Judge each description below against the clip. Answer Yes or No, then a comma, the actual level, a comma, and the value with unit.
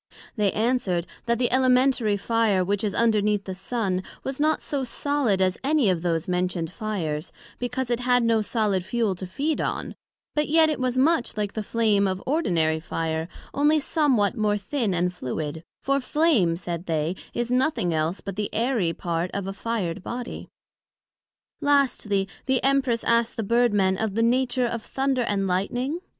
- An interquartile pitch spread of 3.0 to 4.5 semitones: No, wide, 5.4 semitones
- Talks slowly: No, average, 175 wpm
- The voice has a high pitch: Yes, high, 220 Hz